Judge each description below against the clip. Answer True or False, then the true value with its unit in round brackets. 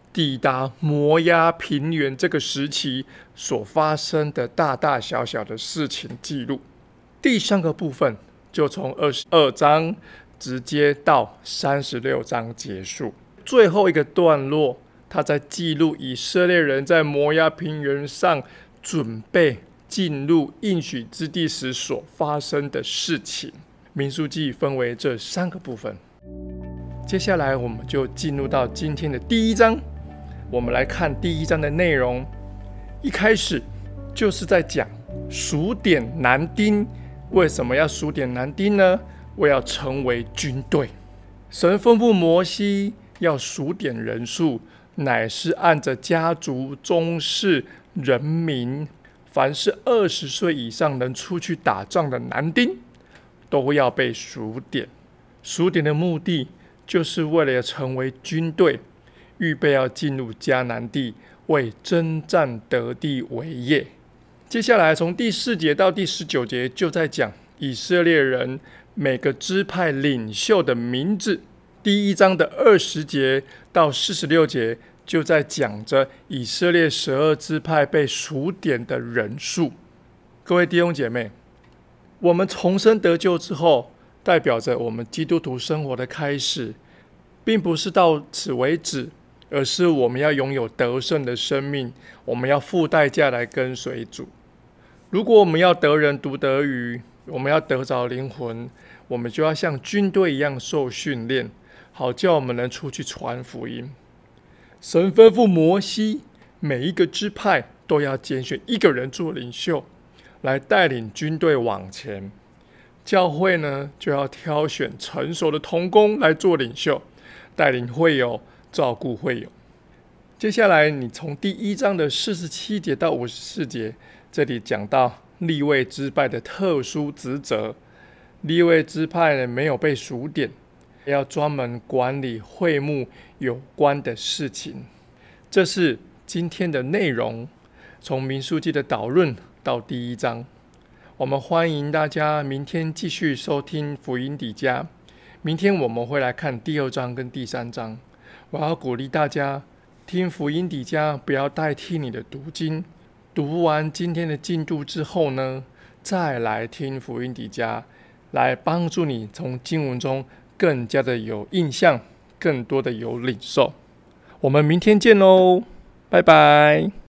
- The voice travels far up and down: False (4.9 semitones)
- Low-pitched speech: False (145 Hz)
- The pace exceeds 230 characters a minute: False (205 characters per minute)